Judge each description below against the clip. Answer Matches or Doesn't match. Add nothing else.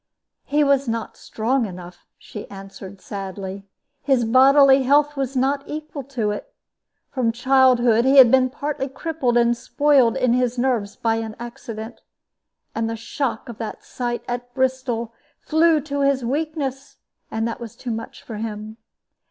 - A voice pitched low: Doesn't match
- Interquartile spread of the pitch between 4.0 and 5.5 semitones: Doesn't match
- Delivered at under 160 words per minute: Matches